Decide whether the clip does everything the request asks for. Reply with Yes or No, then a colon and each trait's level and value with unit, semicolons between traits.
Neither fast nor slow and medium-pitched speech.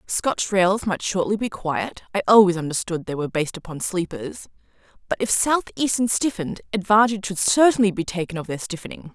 No: average, 170 wpm; high, 195 Hz